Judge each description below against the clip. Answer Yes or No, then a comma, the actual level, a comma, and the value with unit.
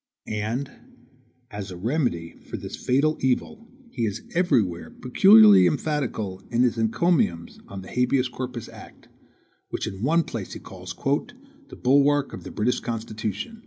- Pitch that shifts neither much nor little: No, wide, 5.9 semitones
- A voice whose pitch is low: Yes, low, 120 Hz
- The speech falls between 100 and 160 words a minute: Yes, average, 145 wpm